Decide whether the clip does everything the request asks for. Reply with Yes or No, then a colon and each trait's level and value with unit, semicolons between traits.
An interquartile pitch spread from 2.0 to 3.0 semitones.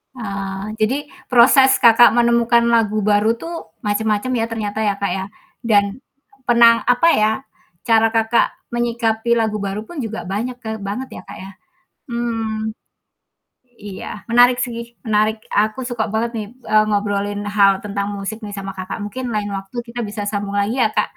Yes: narrow, 2.5 semitones